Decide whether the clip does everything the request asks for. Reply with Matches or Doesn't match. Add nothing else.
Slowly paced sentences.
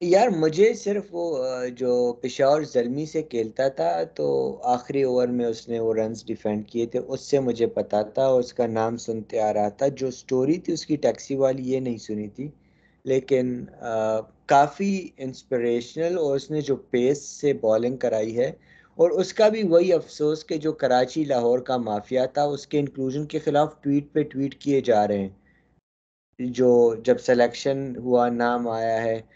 Doesn't match